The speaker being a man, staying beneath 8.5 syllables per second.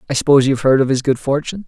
No: male; 8.8 syllables/s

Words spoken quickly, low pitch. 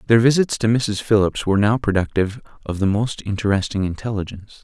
No: average, 170 wpm; low, 105 Hz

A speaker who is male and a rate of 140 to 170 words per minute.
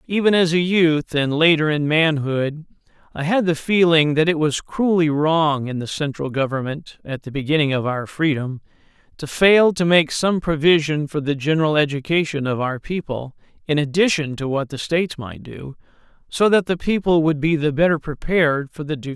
No: male; average, 195 wpm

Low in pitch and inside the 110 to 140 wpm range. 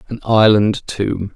Yes: low, 105 Hz; slow, 135 wpm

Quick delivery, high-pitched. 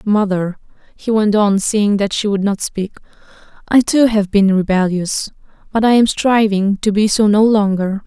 No: average, 180 wpm; high, 205 Hz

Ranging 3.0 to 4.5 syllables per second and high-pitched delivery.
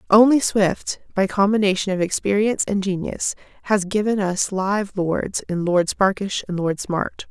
Yes: 4.4 syllables/s; high, 195 Hz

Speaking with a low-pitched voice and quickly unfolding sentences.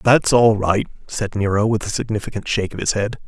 Yes: low, 105 Hz; fast, 220 wpm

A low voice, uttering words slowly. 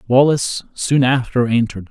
Yes: low, 125 Hz; slow, 125 wpm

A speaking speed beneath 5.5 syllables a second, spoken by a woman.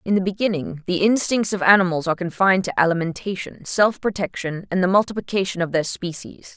No: 6.0 syllables/s; female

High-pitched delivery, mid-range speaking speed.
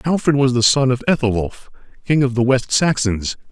No: low, 130 Hz; average, 190 wpm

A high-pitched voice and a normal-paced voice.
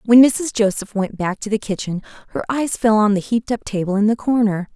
No: high, 215 Hz; fast, 240 wpm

